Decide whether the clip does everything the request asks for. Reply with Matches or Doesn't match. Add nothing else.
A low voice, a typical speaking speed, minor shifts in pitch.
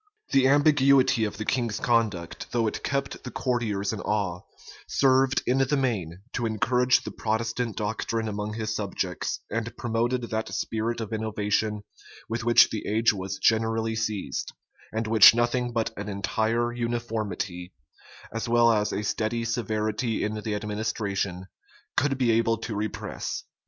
Matches